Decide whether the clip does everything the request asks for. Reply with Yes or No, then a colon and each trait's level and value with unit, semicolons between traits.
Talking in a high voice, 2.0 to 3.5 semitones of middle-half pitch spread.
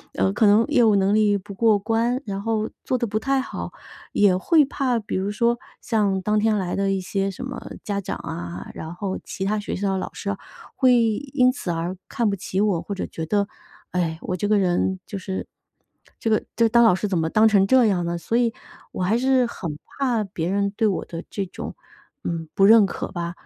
Yes: high, 205 Hz; average, 3.2 semitones